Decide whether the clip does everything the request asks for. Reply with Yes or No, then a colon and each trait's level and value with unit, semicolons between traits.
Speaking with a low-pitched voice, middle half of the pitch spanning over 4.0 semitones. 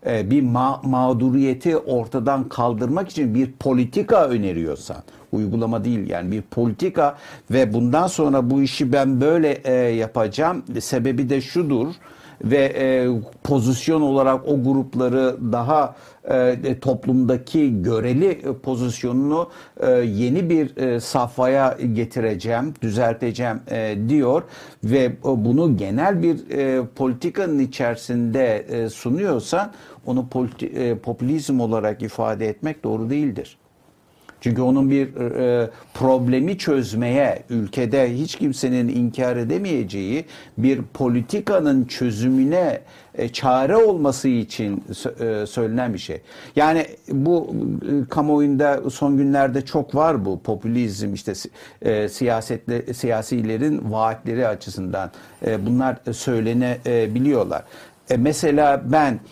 No: low, 125 Hz; average, 2.9 semitones